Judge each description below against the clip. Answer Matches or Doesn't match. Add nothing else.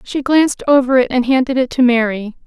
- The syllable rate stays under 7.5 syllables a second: Matches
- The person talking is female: Matches